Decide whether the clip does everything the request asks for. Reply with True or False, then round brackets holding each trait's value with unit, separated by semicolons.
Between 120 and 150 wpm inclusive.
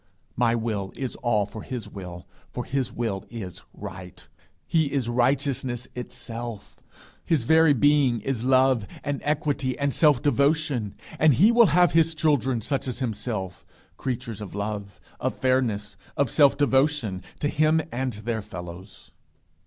True (145 wpm)